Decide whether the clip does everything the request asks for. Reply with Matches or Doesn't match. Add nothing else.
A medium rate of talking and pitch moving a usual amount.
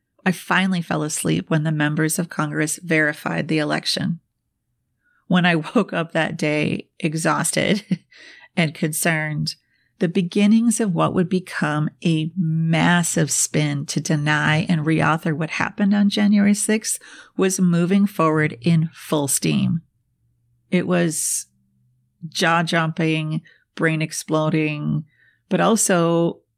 Doesn't match